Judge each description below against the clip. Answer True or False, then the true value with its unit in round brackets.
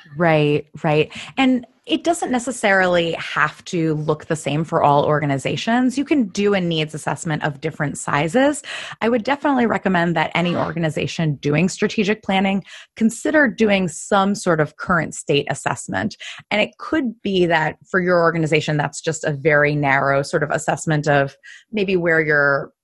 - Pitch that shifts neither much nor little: False (5.9 semitones)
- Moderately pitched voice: True (165 Hz)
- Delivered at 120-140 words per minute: False (160 wpm)